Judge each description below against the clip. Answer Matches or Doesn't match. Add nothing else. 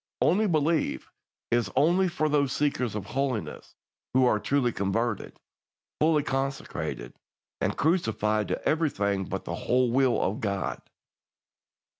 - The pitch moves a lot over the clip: Matches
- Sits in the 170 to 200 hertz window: Doesn't match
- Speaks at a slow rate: Matches